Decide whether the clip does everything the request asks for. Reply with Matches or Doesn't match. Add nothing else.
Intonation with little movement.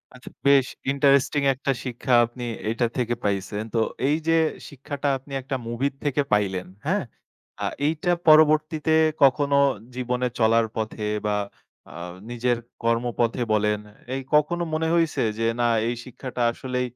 Doesn't match